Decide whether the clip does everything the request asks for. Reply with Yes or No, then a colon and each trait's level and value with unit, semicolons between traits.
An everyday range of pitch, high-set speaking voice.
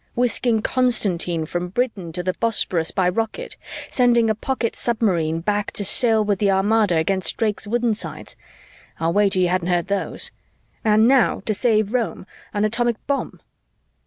Yes: average, 4.0 semitones; high, 210 Hz